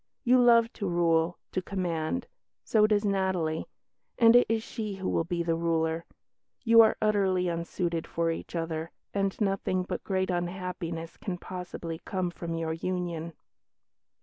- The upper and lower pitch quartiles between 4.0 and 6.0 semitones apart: No, average, 3.0 semitones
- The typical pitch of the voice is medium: Yes, medium, 180 Hz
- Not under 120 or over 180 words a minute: Yes, average, 150 wpm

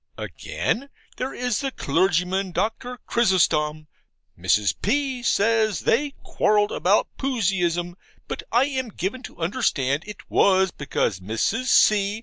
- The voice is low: No, high, 200 Hz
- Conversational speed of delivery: No, slow, 125 wpm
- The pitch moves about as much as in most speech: No, wide, 6.2 semitones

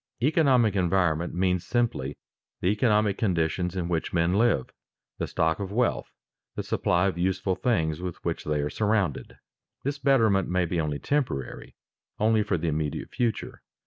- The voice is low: Yes, very low, 95 Hz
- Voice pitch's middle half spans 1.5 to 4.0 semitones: No, average, 4.9 semitones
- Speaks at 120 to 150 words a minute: No, average, 160 wpm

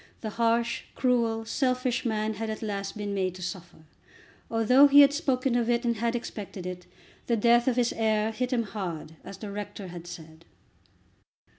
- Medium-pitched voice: No, high, 225 Hz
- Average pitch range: Yes, average, 3.3 semitones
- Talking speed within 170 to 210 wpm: Yes, average, 180 wpm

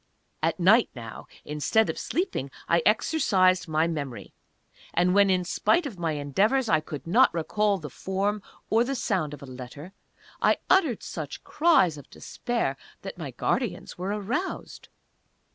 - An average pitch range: No, wide, 6.3 semitones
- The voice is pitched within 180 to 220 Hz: Yes, medium, 185 Hz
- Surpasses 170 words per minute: No, average, 155 wpm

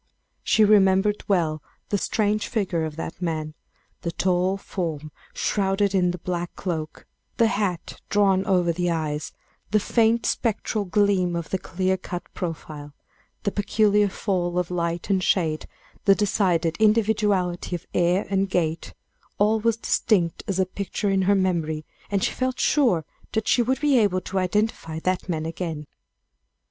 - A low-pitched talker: No, medium, 185 Hz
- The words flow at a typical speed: Yes, average, 155 wpm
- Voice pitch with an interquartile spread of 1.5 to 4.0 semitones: Yes, average, 3.3 semitones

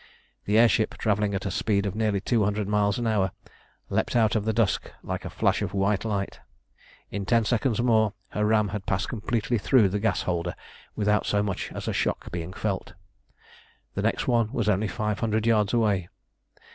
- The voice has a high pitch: No, low, 105 Hz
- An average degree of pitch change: No, narrow, 1.9 semitones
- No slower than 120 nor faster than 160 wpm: No, average, 195 wpm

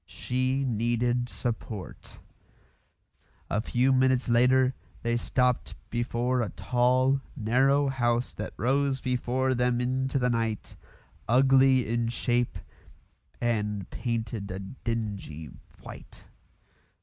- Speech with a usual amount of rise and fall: No, narrow, 2.0 semitones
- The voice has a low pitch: Yes, low, 125 Hz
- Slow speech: Yes, slow, 100 wpm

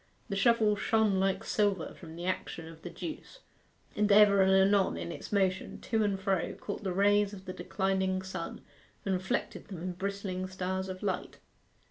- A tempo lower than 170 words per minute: No, average, 180 wpm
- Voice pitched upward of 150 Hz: Yes, high, 190 Hz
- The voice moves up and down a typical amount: No, narrow, 1.6 semitones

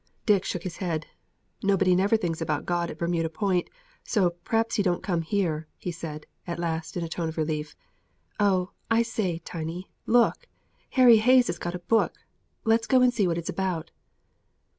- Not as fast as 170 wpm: No, average, 185 wpm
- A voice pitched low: No, medium, 180 Hz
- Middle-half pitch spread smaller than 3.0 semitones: No, average, 4.5 semitones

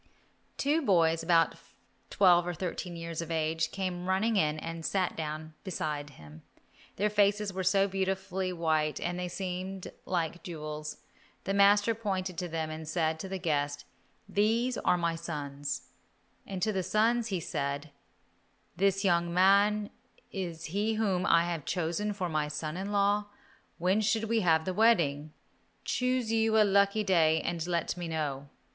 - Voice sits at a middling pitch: Yes, medium, 180 Hz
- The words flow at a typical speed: Yes, average, 160 wpm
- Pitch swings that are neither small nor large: Yes, average, 3.8 semitones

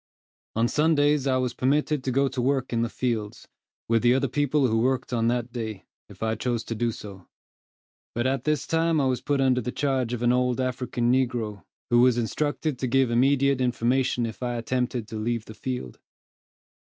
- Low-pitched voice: Yes, low, 125 Hz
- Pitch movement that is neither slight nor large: No, narrow, 2.3 semitones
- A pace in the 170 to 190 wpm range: No, average, 200 wpm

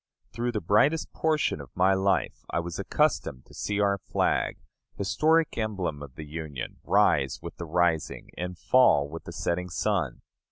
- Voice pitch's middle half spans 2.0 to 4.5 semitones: No, average, 5.1 semitones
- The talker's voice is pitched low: Yes, very low, 90 Hz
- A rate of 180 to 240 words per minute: No, average, 165 wpm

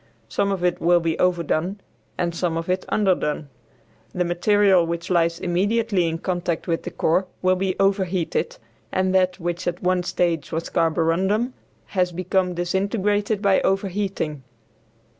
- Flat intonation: Yes, narrow, 2.3 semitones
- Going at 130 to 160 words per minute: Yes, average, 145 wpm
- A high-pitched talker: No, medium, 180 Hz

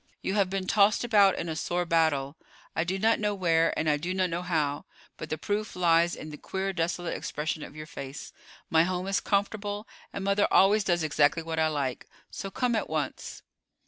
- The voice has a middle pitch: Yes, medium, 175 Hz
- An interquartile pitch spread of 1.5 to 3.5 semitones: No, average, 3.9 semitones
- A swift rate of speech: Yes, fast, 210 wpm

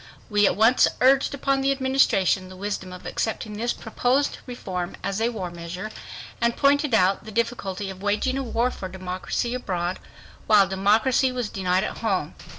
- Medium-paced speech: Yes, average, 170 wpm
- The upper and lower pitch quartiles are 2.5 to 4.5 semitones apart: No, average, 4.9 semitones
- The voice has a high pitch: Yes, high, 215 Hz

